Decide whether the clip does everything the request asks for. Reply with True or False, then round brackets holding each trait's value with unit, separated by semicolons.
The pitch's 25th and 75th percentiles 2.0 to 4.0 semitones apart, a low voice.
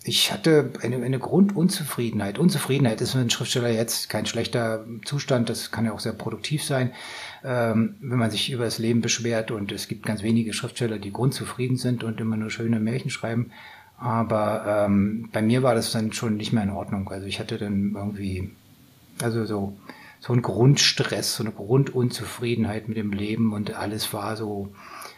True (2.5 semitones; 115 Hz)